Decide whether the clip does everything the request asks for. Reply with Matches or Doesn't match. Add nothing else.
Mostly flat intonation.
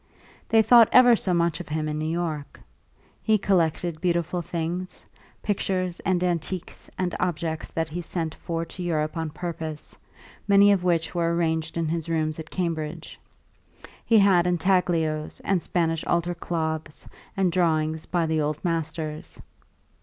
Matches